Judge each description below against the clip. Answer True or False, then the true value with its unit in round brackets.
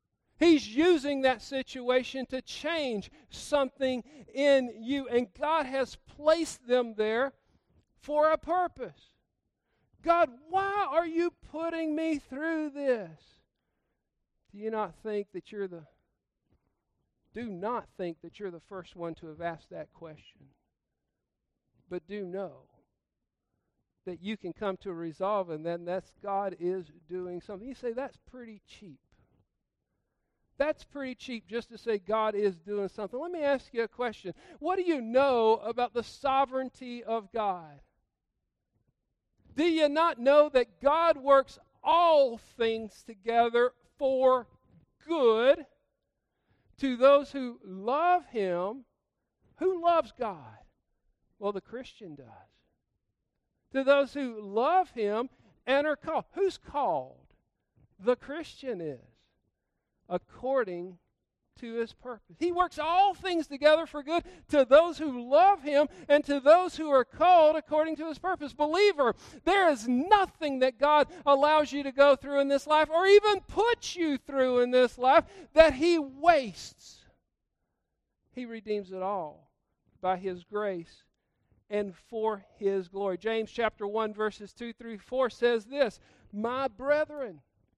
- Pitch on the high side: True (255 Hz)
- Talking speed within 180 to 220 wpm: False (140 wpm)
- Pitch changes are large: True (6.5 semitones)